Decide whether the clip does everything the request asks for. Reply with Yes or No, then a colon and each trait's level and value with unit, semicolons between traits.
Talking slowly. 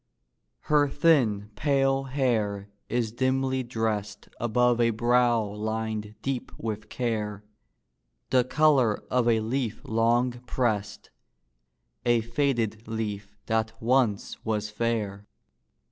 Yes: slow, 105 wpm